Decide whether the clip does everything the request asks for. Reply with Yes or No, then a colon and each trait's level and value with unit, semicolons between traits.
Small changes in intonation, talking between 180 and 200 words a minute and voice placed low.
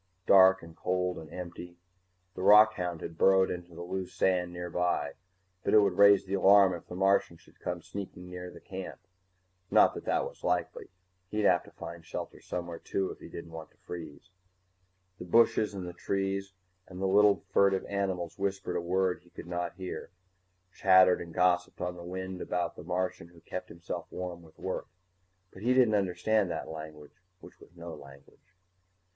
Yes: narrow, 1.9 semitones; average, 185 wpm; very low, 90 Hz